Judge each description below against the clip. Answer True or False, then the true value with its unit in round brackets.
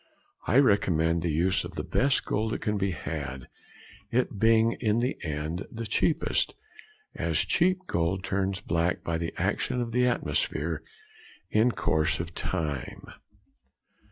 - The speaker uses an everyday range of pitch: False (5.8 semitones)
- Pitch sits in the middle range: False (95 Hz)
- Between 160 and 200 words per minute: False (145 wpm)